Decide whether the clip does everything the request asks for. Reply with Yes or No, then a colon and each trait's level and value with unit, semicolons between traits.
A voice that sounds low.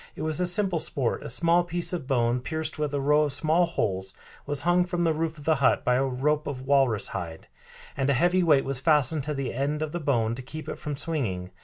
No: medium, 145 Hz